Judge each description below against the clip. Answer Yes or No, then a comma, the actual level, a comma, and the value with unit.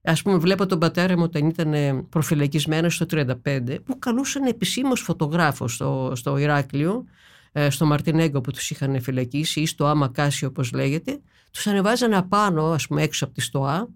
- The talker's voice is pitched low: No, medium, 155 Hz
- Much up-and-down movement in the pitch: No, average, 4.3 semitones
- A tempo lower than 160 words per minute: No, fast, 170 wpm